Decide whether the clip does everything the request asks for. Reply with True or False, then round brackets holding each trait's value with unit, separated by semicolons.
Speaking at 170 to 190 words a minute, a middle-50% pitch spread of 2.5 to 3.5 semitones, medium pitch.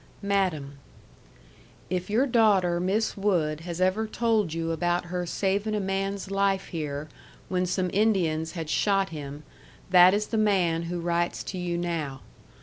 False (150 wpm; 3.1 semitones; 180 Hz)